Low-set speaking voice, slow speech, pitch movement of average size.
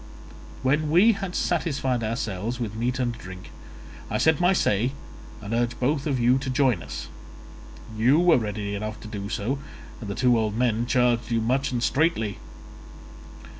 No: low, 120 Hz; average, 170 wpm; average, 3.9 semitones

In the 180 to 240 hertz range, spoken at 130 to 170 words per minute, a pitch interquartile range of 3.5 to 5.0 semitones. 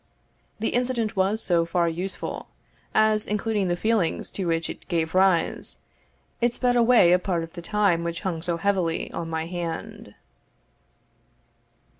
Yes: medium, 185 Hz; average, 150 wpm; average, 4.1 semitones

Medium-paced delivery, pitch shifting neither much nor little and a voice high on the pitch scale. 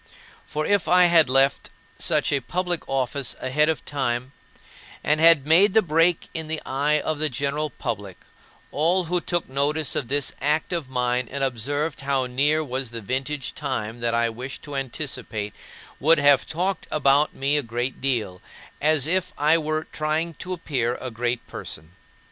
No: average, 170 wpm; average, 3.7 semitones; medium, 140 Hz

